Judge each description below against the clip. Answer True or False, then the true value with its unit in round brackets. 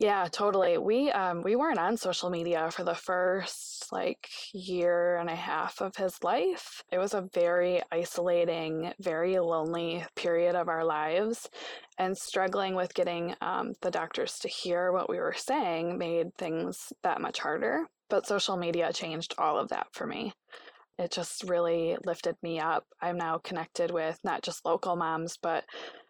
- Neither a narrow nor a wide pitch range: False (1.8 semitones)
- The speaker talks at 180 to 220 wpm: False (170 wpm)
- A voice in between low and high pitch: True (175 Hz)